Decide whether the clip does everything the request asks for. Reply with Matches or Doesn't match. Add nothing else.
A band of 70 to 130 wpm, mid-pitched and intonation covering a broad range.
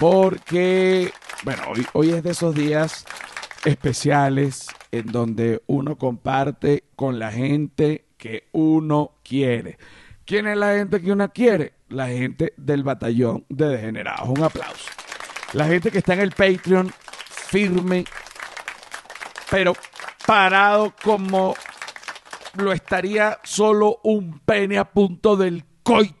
Matches